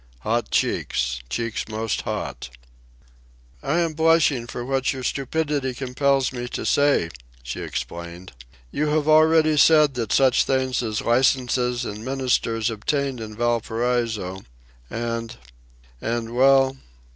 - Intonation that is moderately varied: Yes, average, 3.3 semitones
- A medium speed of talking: No, slow, 120 wpm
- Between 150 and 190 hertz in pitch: No, low, 125 Hz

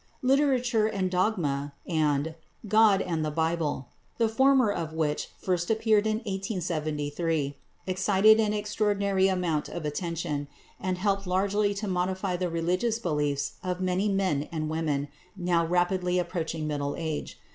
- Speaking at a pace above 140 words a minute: No, slow, 135 wpm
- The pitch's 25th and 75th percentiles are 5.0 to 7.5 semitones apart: No, average, 4.2 semitones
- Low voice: No, medium, 180 Hz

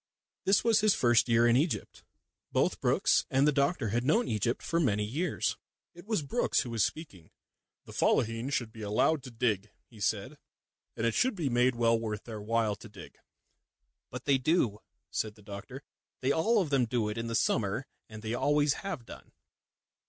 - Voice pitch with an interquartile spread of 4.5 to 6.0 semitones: Yes, average, 5.0 semitones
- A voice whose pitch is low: Yes, low, 120 Hz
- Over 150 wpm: Yes, average, 190 wpm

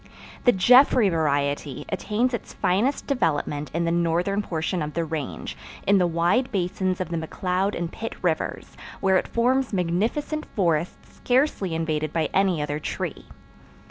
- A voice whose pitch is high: No, medium, 180 Hz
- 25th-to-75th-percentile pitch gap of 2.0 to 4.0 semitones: No, average, 4.4 semitones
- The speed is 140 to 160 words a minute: Yes, average, 150 wpm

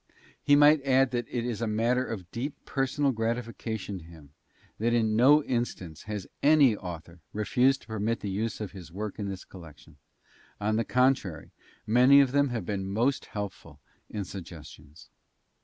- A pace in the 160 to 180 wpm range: Yes, average, 170 wpm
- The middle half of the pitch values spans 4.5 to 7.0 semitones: Yes, average, 4.8 semitones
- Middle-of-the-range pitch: No, low, 110 Hz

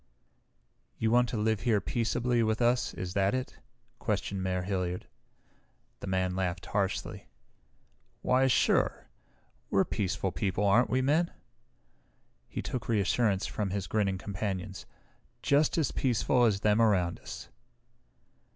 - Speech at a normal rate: No, slow, 130 wpm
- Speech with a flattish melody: No, average, 4.2 semitones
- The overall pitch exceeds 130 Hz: No, low, 105 Hz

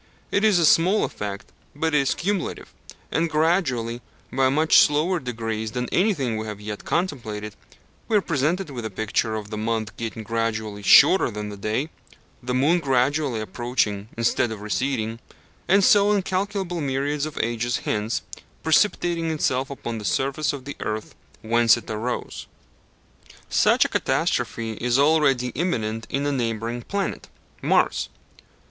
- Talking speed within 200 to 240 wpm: No, average, 150 wpm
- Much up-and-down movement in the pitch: Yes, wide, 6.2 semitones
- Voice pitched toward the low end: Yes, low, 125 Hz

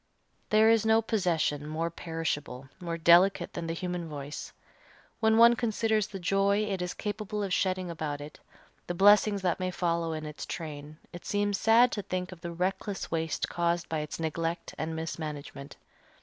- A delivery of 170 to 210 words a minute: Yes, average, 175 wpm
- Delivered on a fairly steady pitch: No, average, 4.0 semitones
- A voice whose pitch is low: No, medium, 175 Hz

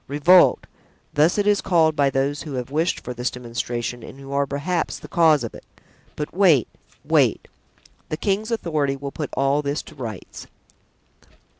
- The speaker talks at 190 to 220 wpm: No, average, 170 wpm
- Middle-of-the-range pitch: Yes, medium, 145 Hz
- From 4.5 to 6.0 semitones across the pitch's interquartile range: No, average, 3.5 semitones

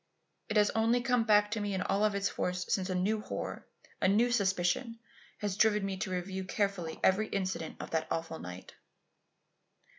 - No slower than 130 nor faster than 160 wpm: No, average, 180 wpm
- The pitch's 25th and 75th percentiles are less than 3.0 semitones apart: Yes, narrow, 2.6 semitones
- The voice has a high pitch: Yes, high, 200 Hz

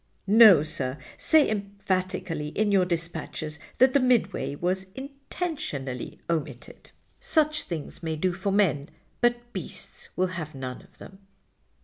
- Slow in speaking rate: Yes, slow, 130 wpm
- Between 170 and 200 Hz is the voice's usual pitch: Yes, medium, 185 Hz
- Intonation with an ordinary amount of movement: No, wide, 5.9 semitones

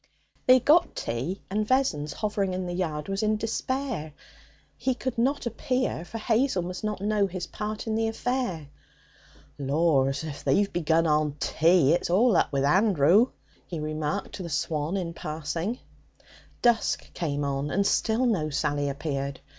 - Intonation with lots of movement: Yes, wide, 6.5 semitones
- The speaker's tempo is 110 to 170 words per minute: Yes, average, 160 wpm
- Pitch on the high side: No, medium, 180 Hz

